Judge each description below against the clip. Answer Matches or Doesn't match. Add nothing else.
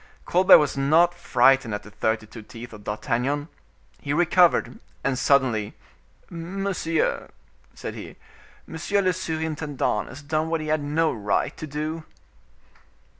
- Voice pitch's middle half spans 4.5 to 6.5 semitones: Matches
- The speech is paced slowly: Matches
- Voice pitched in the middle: Matches